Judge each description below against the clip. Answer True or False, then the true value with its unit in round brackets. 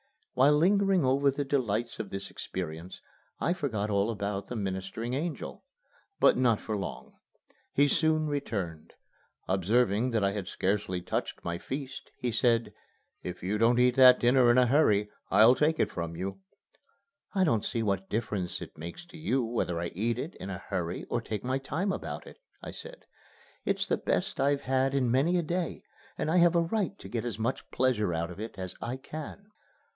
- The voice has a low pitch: True (120 Hz)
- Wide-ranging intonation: True (6.2 semitones)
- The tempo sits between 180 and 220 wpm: True (190 wpm)